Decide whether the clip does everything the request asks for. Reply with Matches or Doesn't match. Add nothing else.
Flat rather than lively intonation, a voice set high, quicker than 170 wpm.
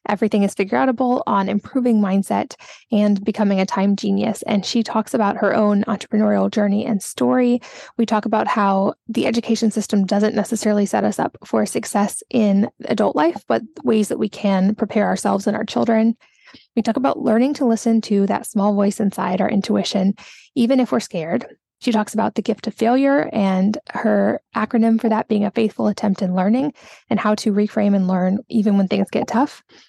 Matches